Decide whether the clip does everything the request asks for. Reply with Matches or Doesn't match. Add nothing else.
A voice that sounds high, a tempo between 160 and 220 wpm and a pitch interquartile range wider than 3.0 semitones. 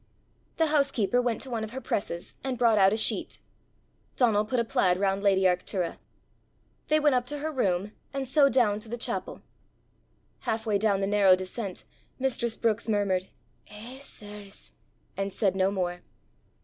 Matches